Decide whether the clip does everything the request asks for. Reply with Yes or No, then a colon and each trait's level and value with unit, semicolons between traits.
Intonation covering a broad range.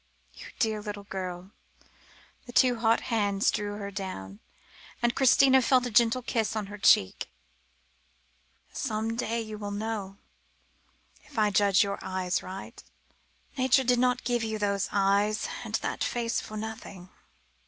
No: average, 2.9 semitones